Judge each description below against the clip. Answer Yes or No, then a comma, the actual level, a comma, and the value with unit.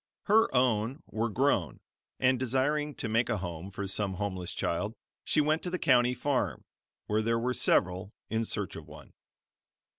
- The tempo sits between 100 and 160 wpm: No, average, 170 wpm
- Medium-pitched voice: No, low, 115 Hz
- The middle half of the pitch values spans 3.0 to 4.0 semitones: No, average, 4.5 semitones